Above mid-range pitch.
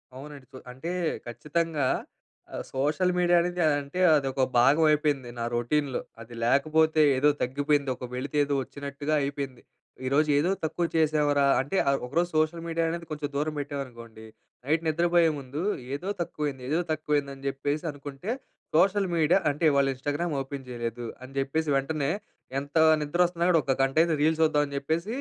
No: medium, 145 Hz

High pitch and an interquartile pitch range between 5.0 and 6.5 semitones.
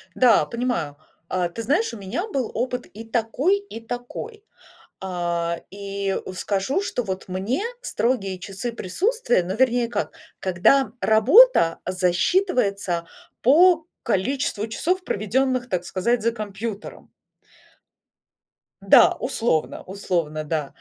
Yes: high, 220 Hz; wide, 5.6 semitones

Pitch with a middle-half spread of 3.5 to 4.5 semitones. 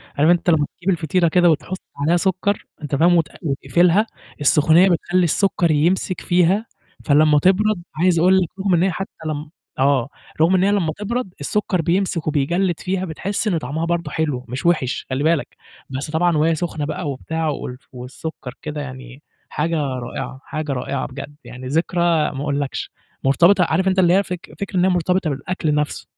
Yes: average, 3.9 semitones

